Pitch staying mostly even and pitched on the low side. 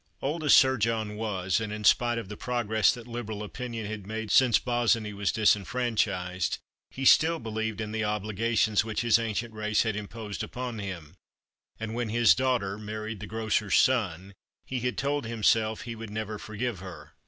Yes: narrow, 2.2 semitones; low, 110 Hz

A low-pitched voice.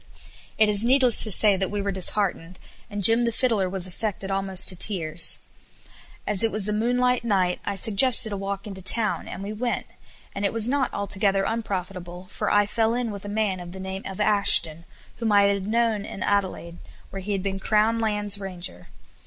No: high, 200 Hz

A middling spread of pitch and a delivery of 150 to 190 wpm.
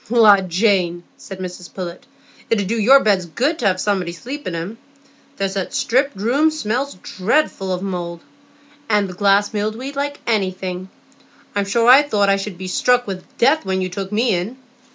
Yes: average, 4.2 semitones; average, 185 wpm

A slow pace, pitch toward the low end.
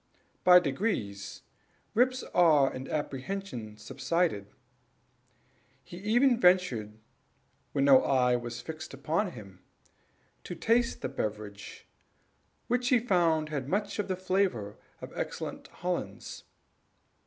No: slow, 110 wpm; medium, 160 Hz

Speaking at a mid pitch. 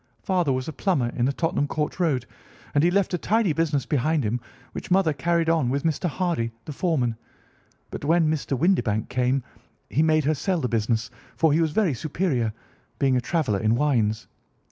Yes: medium, 150 Hz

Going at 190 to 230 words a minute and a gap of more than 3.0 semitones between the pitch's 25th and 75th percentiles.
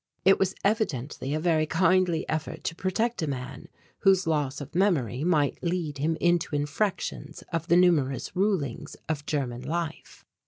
No: average, 155 wpm; average, 4.1 semitones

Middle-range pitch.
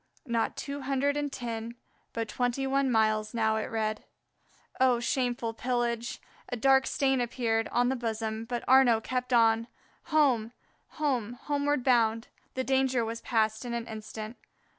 No: high, 240 Hz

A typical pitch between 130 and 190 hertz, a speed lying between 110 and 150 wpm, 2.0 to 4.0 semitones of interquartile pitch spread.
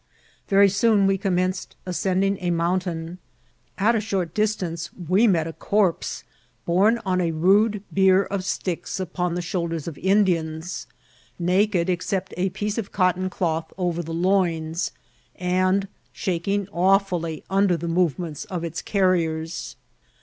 Yes: medium, 185 Hz; slow, 135 wpm; narrow, 2.5 semitones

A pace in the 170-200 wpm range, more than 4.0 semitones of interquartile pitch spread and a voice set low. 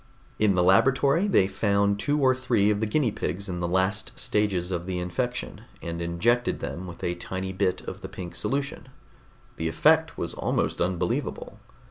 Yes: average, 175 wpm; wide, 5.5 semitones; low, 100 Hz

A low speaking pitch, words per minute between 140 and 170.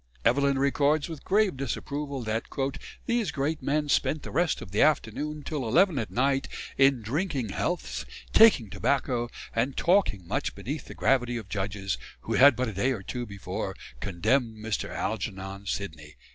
Yes: low, 130 Hz; average, 160 wpm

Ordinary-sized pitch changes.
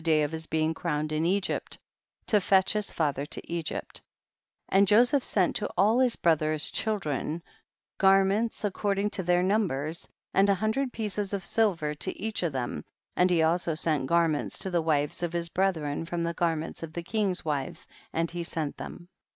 Yes: average, 4.0 semitones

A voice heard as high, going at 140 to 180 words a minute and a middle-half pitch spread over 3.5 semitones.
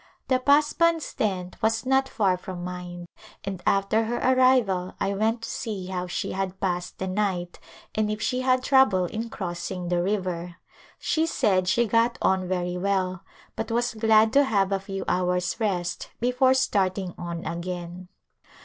Yes: high, 195 Hz; average, 165 wpm; average, 4.2 semitones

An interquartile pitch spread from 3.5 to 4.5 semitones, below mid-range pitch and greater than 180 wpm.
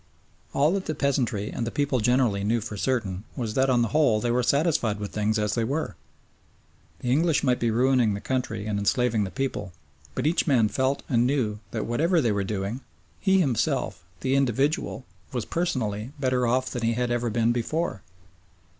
Yes: average, 3.9 semitones; low, 120 Hz; average, 190 wpm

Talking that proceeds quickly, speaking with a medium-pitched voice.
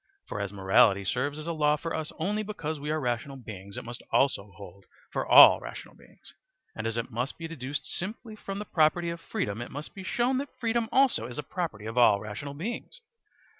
Yes: fast, 215 wpm; medium, 145 Hz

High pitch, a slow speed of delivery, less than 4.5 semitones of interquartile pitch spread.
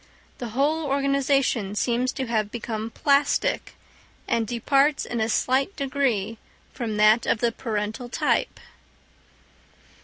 Yes: high, 240 Hz; slow, 120 wpm; average, 3.9 semitones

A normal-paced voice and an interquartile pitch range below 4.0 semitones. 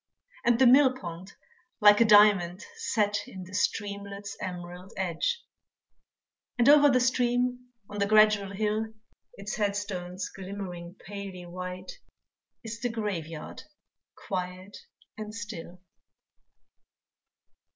No: slow, 110 wpm; average, 3.3 semitones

